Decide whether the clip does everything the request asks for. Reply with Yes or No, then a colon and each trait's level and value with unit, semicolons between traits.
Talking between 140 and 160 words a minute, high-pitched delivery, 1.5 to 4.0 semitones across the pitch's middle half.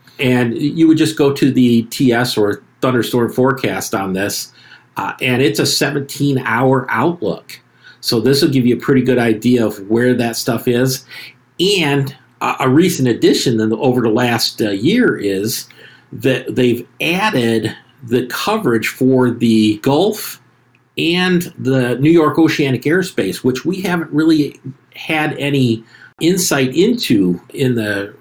No: average, 150 wpm; low, 125 Hz; average, 3.4 semitones